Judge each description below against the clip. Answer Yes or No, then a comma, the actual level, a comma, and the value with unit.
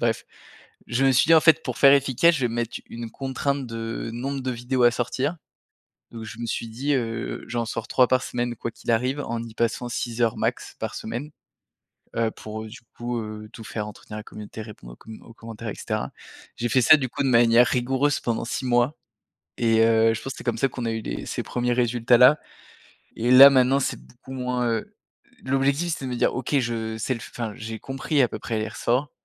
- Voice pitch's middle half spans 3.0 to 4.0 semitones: No, narrow, 2.5 semitones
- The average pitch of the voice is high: No, low, 120 Hz